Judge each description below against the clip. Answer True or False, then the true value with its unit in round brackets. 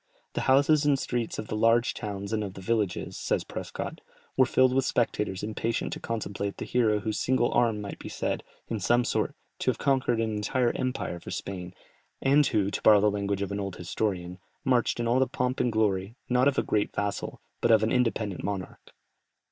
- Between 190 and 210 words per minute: True (205 wpm)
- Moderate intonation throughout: True (3.5 semitones)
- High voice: False (110 Hz)